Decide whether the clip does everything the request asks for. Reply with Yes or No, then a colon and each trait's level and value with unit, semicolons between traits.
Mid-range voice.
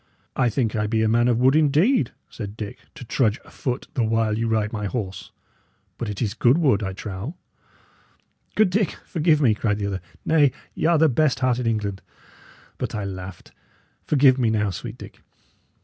No: low, 115 Hz